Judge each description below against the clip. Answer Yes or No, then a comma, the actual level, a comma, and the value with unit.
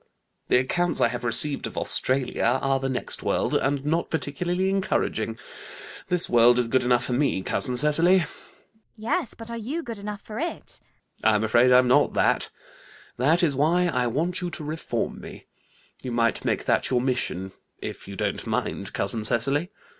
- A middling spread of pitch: No, wide, 6.3 semitones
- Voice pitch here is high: No, low, 135 Hz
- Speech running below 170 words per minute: No, average, 180 wpm